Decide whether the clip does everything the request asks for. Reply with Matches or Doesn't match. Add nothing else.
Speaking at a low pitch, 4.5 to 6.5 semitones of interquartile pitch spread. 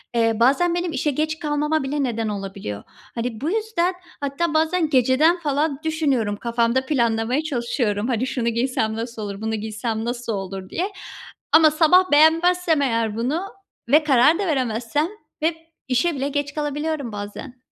Doesn't match